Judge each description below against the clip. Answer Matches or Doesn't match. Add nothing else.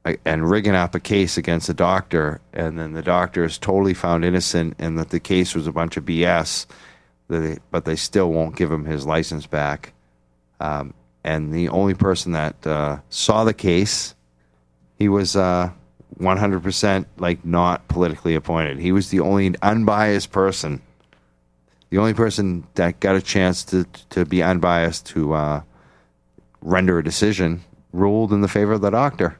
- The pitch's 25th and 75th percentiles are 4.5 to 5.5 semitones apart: Doesn't match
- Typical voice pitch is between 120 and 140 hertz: Doesn't match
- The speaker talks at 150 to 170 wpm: Matches